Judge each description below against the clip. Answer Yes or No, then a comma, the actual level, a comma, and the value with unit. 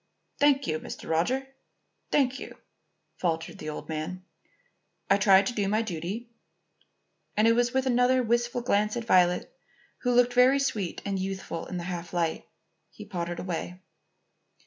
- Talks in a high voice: Yes, high, 205 Hz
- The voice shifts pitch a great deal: Yes, wide, 5.7 semitones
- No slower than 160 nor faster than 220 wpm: No, average, 145 wpm